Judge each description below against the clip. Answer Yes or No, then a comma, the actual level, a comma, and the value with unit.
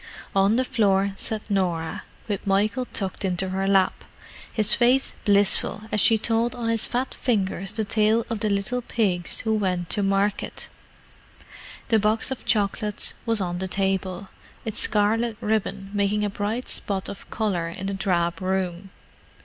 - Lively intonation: No, narrow, 2.5 semitones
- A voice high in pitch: Yes, high, 205 Hz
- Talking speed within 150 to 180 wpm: Yes, average, 160 wpm